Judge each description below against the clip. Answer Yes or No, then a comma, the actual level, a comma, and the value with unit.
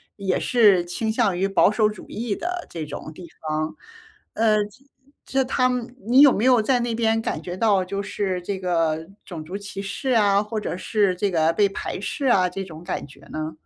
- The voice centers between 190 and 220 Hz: Yes, high, 200 Hz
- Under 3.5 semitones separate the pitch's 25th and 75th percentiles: No, average, 4.1 semitones